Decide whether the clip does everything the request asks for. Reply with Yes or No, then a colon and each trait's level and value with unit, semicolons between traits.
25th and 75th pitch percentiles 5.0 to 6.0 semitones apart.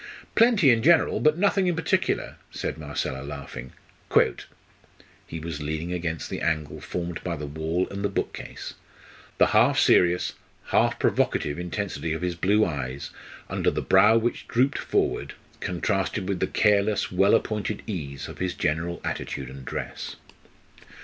Yes: average, 5.3 semitones